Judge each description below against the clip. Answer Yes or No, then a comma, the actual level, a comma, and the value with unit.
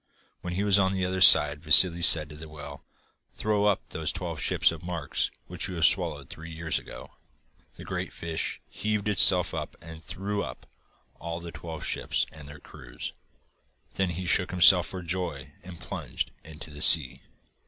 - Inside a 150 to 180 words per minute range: Yes, average, 175 wpm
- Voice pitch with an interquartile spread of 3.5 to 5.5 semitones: No, average, 3.1 semitones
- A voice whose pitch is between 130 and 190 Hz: No, very low, 85 Hz